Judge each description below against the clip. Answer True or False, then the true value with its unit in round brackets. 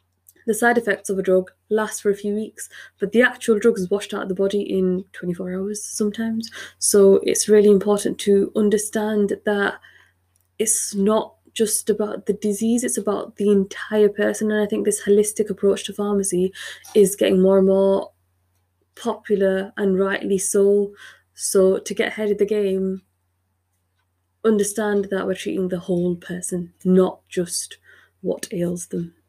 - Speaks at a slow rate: False (160 wpm)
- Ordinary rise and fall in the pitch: False (2.3 semitones)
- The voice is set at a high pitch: True (200 Hz)